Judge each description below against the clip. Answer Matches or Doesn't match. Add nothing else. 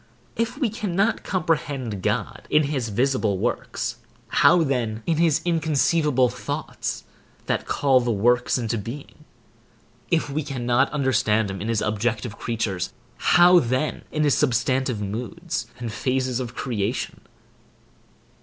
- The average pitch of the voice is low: Matches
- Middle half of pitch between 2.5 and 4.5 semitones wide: Doesn't match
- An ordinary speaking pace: Doesn't match